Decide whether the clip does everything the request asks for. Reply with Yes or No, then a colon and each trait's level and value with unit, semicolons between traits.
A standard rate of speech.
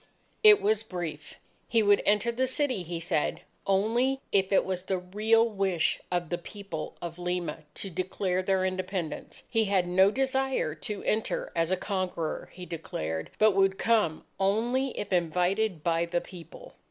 Yes: average, 165 wpm